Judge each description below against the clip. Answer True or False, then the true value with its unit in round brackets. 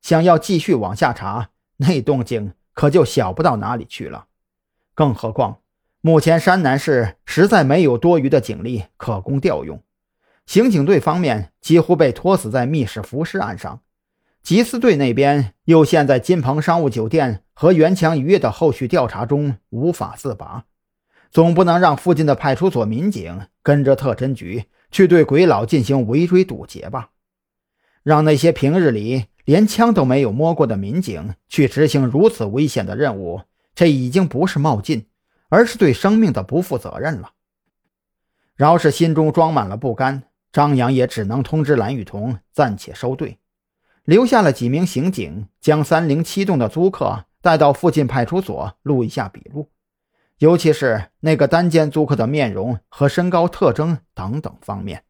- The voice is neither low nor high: True (145 Hz)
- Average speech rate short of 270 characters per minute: True (250 characters per minute)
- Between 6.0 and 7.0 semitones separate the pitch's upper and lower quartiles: False (5.2 semitones)